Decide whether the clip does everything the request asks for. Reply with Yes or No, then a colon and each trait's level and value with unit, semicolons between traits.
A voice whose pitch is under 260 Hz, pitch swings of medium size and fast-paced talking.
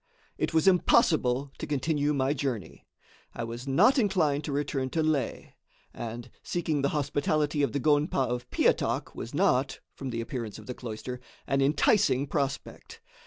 No: medium, 140 Hz; average, 3.3 semitones; average, 160 wpm